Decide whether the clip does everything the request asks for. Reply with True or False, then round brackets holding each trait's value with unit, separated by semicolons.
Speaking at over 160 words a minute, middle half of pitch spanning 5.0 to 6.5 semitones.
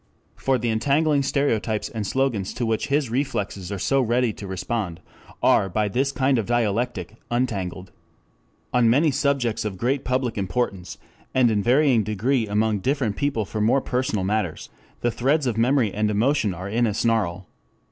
False (170 wpm; 4.2 semitones)